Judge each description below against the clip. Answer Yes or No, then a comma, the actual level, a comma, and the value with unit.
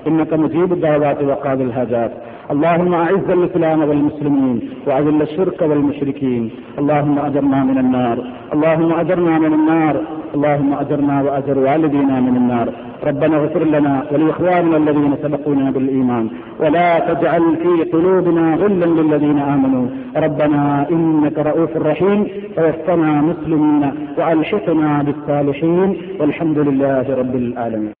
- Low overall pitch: No, medium, 150 Hz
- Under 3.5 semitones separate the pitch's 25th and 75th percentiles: Yes, average, 2.8 semitones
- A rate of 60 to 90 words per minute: No, average, 110 wpm